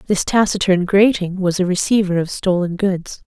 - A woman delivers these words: Yes, female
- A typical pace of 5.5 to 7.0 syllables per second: No, 4.9 syllables/s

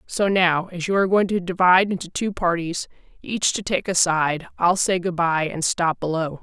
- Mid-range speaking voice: Yes, medium, 175 Hz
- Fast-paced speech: Yes, fast, 215 wpm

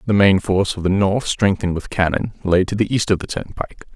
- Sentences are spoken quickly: Yes, fast, 245 wpm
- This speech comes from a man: Yes, male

